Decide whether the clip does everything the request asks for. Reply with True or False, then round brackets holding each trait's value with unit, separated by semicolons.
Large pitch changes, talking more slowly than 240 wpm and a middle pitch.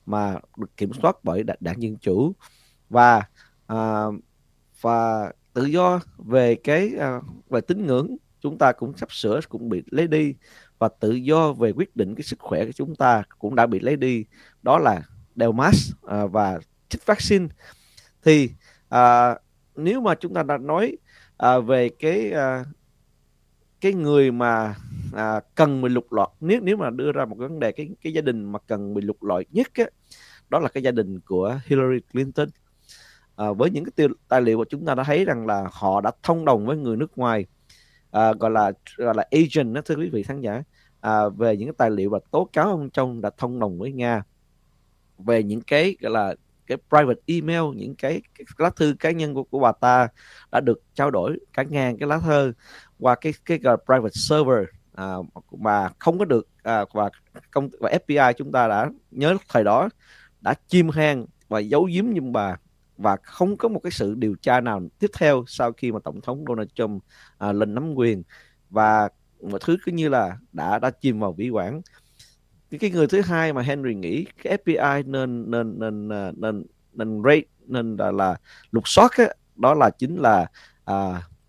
False (6.0 semitones; 195 wpm; 125 Hz)